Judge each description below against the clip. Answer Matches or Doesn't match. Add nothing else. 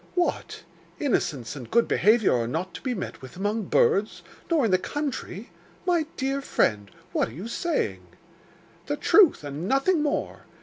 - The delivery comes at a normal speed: Matches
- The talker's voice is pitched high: Matches